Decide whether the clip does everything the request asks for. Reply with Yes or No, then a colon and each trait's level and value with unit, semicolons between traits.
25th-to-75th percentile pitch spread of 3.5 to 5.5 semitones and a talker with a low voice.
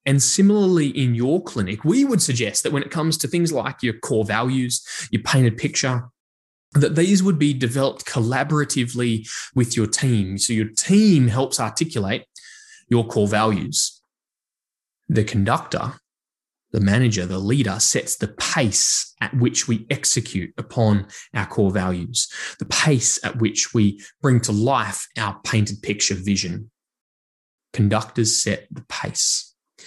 Yes: average, 4.5 semitones; low, 120 Hz